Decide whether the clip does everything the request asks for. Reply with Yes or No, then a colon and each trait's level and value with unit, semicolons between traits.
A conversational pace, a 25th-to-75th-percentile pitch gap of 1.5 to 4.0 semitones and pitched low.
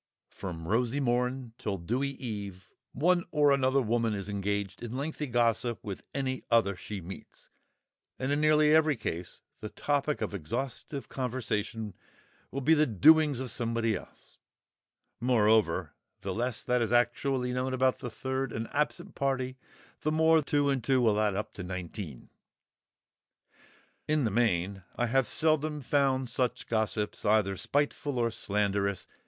No: average, 150 wpm; average, 4.8 semitones; low, 120 Hz